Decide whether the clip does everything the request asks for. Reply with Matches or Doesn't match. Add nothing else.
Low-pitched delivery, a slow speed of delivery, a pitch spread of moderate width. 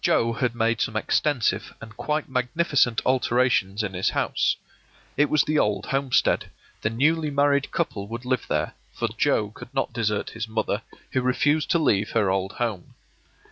Doesn't match